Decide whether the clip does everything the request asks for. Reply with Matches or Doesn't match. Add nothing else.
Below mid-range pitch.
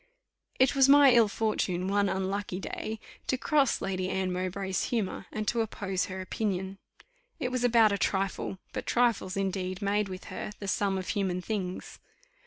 Doesn't match